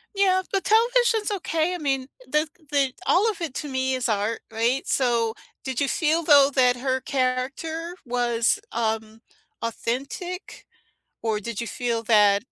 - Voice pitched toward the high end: Yes, very high, 260 Hz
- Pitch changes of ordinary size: No, wide, 5.8 semitones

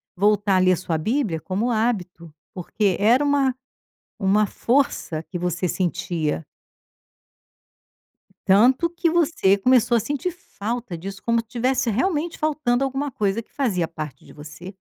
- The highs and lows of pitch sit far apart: Yes, wide, 6.4 semitones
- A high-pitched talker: Yes, high, 215 Hz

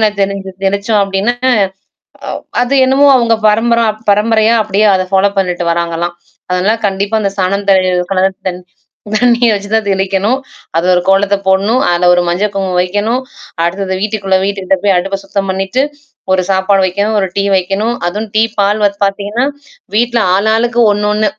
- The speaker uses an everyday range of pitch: No, narrow, 2.2 semitones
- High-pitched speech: Yes, high, 200 Hz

